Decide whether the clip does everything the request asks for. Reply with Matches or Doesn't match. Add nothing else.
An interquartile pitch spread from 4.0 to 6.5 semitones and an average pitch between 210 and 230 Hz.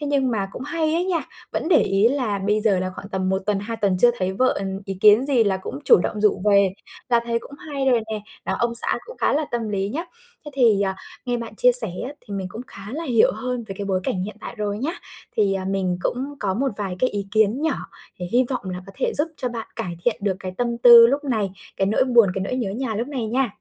Matches